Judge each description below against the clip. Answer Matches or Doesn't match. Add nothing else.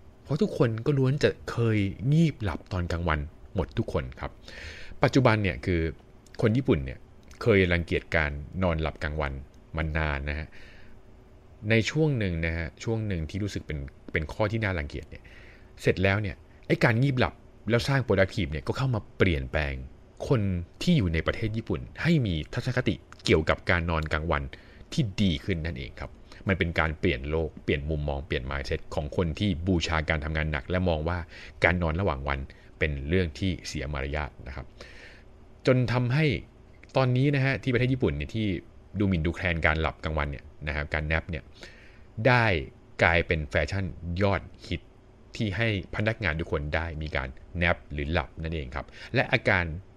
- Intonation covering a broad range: Matches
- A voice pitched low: Matches